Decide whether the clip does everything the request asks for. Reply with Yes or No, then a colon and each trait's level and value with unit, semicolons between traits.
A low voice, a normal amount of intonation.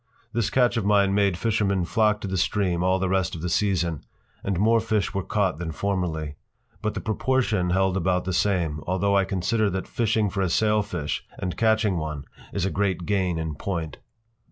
Yes: very low, 95 Hz; average, 3.1 semitones